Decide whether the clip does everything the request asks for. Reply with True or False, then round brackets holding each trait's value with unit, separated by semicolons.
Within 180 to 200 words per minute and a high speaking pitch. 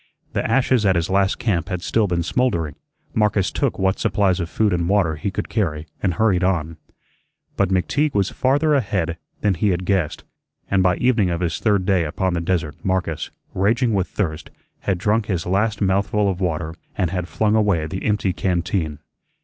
False (190 wpm; 95 Hz)